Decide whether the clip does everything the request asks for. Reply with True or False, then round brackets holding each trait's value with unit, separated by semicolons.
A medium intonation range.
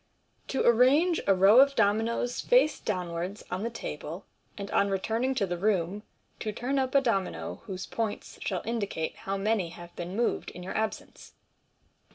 True (4.2 semitones)